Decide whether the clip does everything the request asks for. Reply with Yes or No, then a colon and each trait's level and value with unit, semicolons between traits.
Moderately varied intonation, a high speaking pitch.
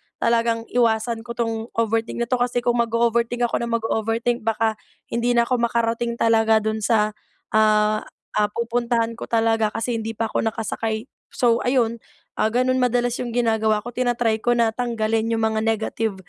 No: narrow, 1.2 semitones; high, 230 Hz